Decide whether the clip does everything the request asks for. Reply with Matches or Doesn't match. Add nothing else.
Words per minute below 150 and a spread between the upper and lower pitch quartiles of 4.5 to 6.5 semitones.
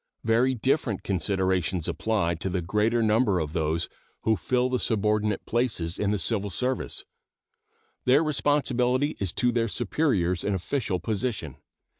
Matches